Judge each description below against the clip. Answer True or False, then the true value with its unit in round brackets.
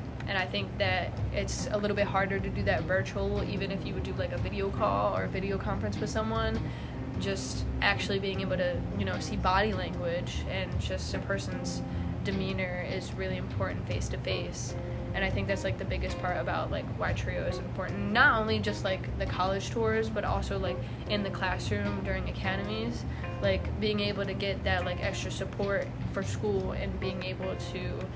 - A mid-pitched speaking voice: False (95 Hz)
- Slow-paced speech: False (200 wpm)